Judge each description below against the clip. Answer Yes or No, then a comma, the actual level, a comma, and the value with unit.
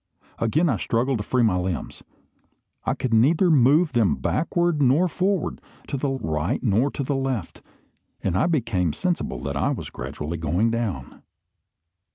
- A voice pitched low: Yes, low, 120 Hz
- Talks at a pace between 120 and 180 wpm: Yes, average, 160 wpm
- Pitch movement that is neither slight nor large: No, wide, 8.2 semitones